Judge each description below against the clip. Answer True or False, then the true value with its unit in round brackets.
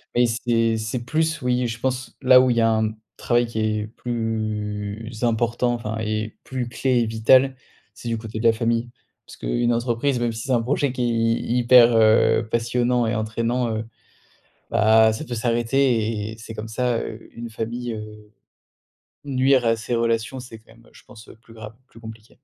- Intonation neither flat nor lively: False (1.7 semitones)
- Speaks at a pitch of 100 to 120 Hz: True (115 Hz)